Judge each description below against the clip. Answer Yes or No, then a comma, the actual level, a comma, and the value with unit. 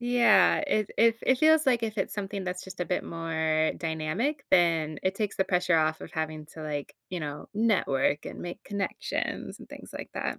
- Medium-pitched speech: Yes, medium, 180 Hz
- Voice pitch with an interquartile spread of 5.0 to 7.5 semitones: Yes, average, 5.3 semitones